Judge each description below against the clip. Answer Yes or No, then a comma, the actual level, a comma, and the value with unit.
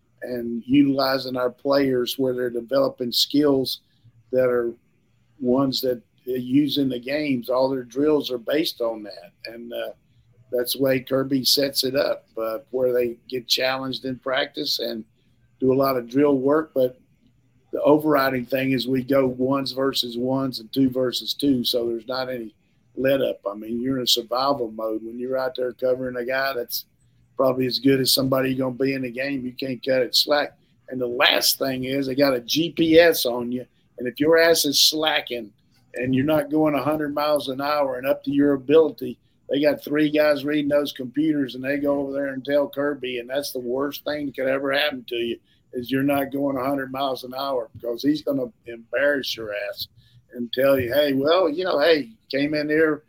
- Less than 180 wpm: No, average, 200 wpm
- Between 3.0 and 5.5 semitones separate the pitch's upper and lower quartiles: No, narrow, 2.5 semitones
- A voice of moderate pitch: No, low, 130 Hz